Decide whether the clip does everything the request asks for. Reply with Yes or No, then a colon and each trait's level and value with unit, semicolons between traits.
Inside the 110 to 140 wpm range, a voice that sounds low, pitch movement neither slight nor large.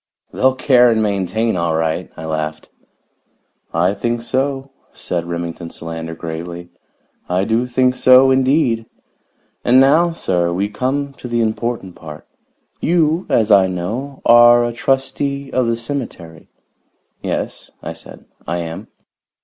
No: slow, 135 wpm; low, 115 Hz; wide, 7.1 semitones